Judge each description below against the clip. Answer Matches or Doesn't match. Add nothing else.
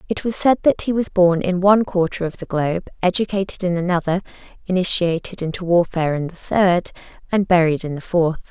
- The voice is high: Doesn't match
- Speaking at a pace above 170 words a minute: Matches